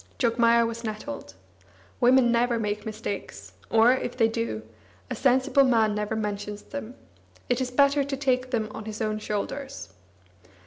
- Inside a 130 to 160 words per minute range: Yes, average, 150 wpm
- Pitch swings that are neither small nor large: Yes, average, 3.1 semitones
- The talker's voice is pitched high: Yes, high, 230 Hz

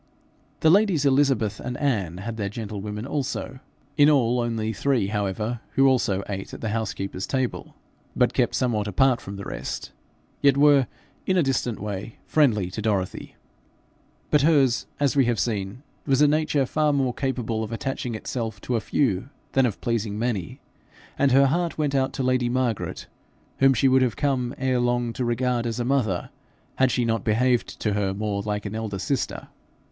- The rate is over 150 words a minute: Yes, average, 180 wpm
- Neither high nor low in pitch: No, low, 120 Hz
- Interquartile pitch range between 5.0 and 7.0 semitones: No, average, 4.1 semitones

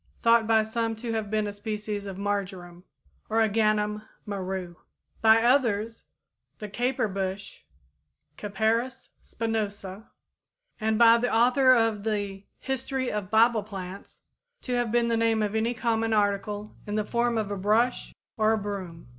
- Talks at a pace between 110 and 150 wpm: Yes, average, 145 wpm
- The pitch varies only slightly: Yes, narrow, 2.1 semitones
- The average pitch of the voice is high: Yes, high, 215 Hz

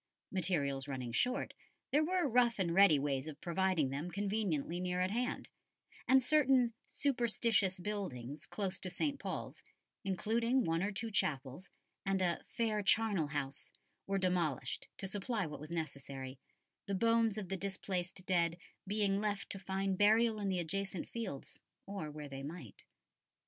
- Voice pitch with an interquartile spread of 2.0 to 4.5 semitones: No, average, 5.3 semitones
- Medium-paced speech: Yes, average, 155 wpm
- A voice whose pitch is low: No, high, 190 Hz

